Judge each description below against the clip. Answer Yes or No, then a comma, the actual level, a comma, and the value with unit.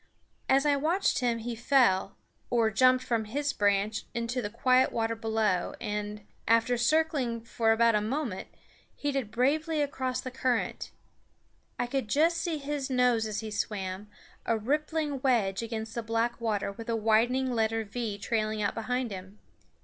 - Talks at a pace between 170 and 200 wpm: No, average, 160 wpm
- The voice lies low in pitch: No, high, 230 Hz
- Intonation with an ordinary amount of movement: Yes, average, 3.2 semitones